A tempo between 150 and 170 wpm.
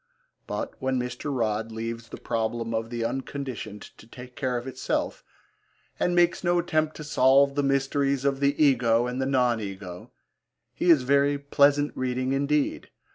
Yes: average, 165 wpm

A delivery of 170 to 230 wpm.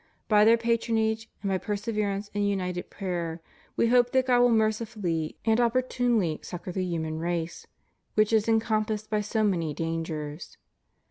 No: average, 155 wpm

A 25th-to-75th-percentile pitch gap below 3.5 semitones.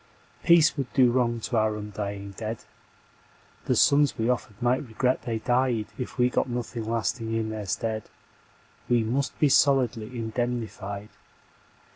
Yes: narrow, 2.4 semitones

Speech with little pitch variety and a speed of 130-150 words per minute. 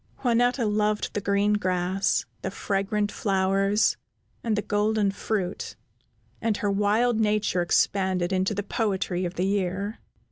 Yes: narrow, 2.0 semitones; slow, 135 wpm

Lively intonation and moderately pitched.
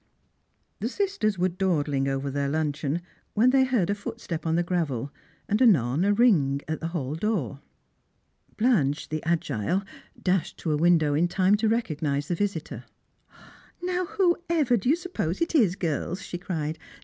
Yes: wide, 6.4 semitones; medium, 175 Hz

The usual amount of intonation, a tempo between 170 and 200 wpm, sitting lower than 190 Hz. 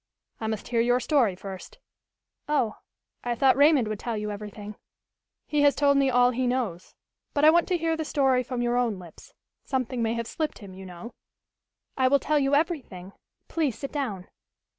No: average, 4.8 semitones; average, 190 wpm; high, 245 Hz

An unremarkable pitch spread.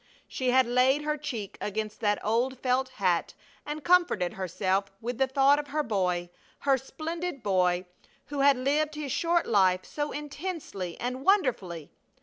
No: wide, 6.7 semitones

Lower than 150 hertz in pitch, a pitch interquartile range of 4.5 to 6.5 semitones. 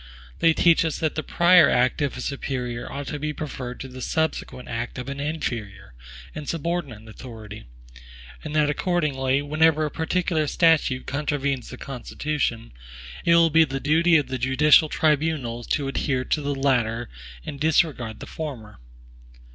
No: medium, 140 Hz; average, 3.8 semitones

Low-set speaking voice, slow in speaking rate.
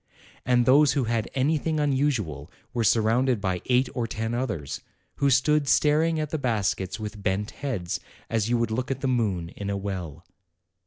No: low, 115 Hz; average, 175 wpm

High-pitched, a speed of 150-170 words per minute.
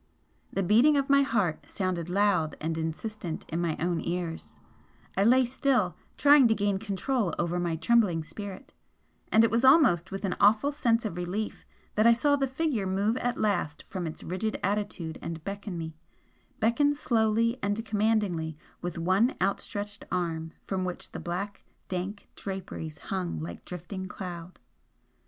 Yes: high, 195 Hz; average, 160 wpm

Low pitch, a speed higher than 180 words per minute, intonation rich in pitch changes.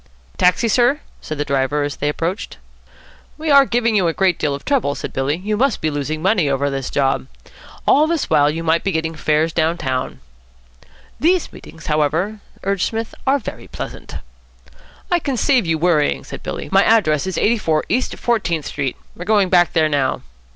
No: medium, 170 Hz; average, 190 wpm; wide, 6.9 semitones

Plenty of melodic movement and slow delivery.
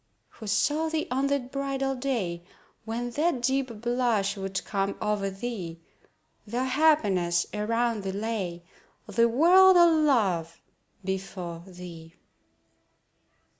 Yes: wide, 5.9 semitones; slow, 115 wpm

